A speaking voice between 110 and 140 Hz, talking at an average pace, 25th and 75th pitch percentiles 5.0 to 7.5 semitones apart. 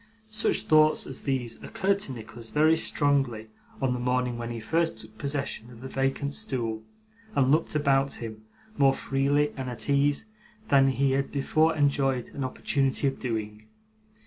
No: low, 135 Hz; average, 165 wpm; average, 3.0 semitones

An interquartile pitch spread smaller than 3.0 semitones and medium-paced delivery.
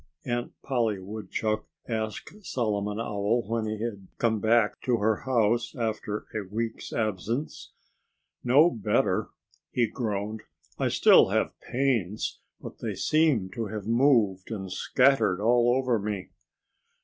No: narrow, 2.5 semitones; slow, 130 wpm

